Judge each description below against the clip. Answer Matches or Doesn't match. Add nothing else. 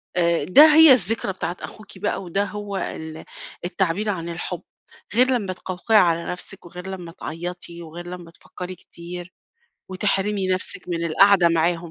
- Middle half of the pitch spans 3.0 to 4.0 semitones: Doesn't match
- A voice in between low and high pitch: Matches